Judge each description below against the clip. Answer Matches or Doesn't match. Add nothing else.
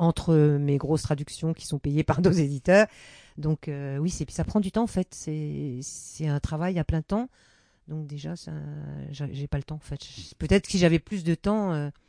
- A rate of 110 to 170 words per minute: Doesn't match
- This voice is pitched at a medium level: Matches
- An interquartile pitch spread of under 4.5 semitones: Matches